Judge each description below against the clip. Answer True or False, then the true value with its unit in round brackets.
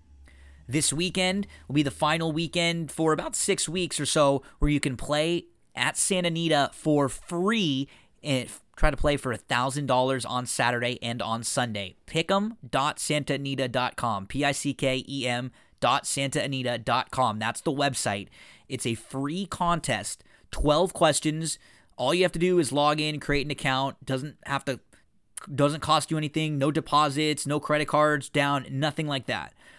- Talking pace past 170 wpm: False (150 wpm)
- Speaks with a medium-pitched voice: True (145 Hz)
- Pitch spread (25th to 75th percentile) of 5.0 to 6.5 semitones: False (3.4 semitones)